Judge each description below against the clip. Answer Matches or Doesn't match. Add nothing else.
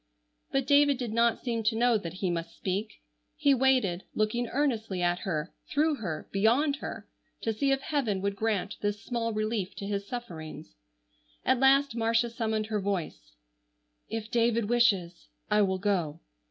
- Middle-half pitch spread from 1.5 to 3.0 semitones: Doesn't match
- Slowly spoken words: Doesn't match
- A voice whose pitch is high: Matches